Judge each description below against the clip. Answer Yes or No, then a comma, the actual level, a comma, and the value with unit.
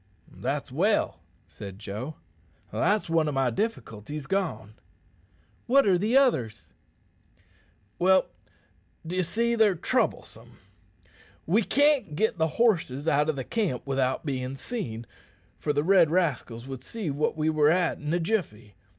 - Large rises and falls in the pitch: Yes, wide, 7.0 semitones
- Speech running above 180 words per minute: No, slow, 135 wpm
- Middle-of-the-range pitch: Yes, medium, 160 Hz